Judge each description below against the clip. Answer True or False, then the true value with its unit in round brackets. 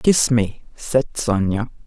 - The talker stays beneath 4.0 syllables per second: True (3.6 syllables/s)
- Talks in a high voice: False (120 Hz)